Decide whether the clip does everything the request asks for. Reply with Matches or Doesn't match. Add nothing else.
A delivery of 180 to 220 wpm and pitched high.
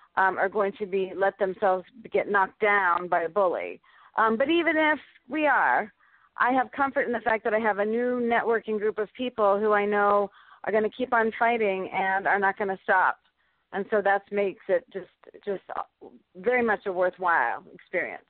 Matches